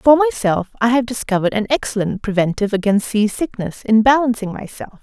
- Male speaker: No, female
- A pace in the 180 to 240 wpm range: No, average, 165 wpm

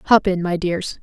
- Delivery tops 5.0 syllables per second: No, 4.1 syllables/s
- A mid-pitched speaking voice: Yes, medium, 180 Hz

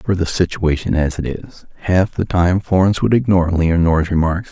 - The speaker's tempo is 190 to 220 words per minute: Yes, average, 200 wpm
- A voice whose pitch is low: Yes, very low, 90 Hz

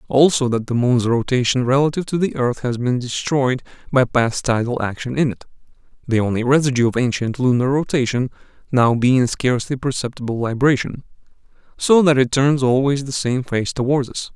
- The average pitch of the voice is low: Yes, low, 130 Hz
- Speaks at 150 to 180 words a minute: Yes, average, 170 wpm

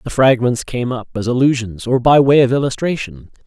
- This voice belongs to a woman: No, male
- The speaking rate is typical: Yes, average, 190 wpm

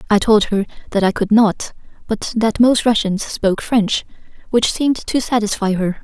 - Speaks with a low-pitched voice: No, high, 215 Hz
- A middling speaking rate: Yes, average, 180 wpm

